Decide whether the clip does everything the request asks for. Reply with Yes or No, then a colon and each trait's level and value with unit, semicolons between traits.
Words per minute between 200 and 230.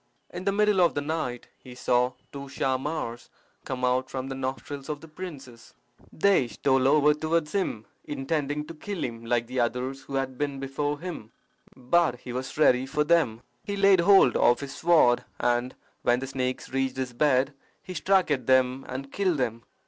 No: average, 185 wpm